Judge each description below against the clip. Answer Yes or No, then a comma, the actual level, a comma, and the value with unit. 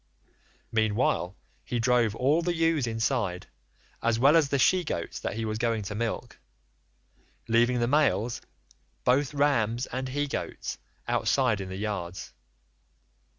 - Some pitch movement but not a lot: Yes, average, 4.2 semitones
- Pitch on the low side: Yes, low, 120 Hz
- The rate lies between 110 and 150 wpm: Yes, average, 140 wpm